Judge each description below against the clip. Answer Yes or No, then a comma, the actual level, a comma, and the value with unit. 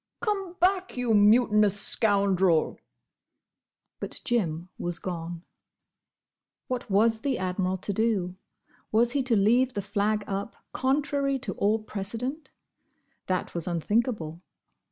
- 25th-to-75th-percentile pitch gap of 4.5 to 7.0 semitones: Yes, average, 5.0 semitones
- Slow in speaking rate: Yes, slow, 115 wpm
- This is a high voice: Yes, high, 215 Hz